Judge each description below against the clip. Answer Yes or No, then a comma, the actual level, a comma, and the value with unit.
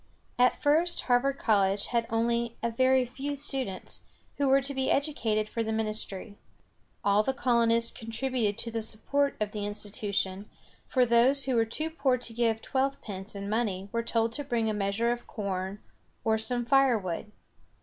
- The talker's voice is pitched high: Yes, high, 230 Hz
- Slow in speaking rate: No, average, 170 wpm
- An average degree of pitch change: Yes, average, 3.7 semitones